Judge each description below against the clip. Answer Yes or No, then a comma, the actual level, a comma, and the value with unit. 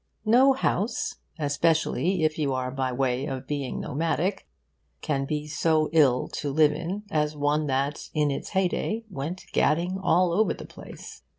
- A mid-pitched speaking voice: Yes, medium, 155 Hz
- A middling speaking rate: Yes, average, 160 wpm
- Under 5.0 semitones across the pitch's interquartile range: Yes, average, 4.0 semitones